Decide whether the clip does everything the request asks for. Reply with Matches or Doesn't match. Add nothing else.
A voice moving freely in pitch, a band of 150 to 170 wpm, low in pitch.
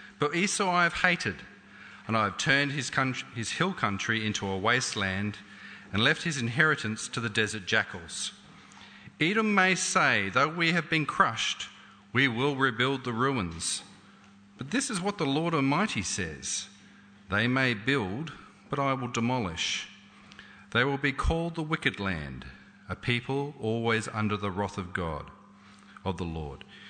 Matches